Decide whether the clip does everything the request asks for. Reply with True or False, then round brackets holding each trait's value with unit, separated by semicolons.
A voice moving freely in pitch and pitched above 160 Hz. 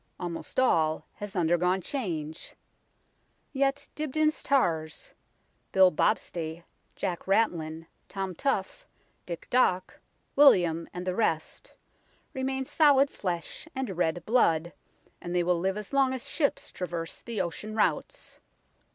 True (7.6 semitones; 185 Hz)